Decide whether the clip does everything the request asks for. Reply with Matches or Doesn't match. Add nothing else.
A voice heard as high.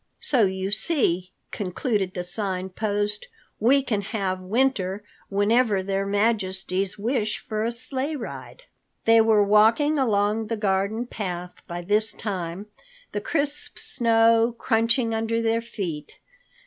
Matches